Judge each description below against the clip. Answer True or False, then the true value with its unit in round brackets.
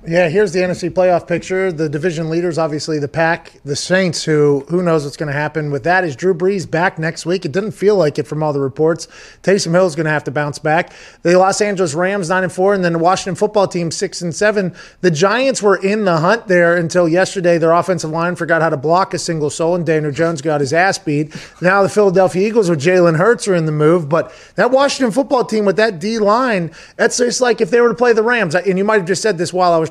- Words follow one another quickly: True (255 wpm)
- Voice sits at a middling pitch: True (180 Hz)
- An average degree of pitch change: True (3.1 semitones)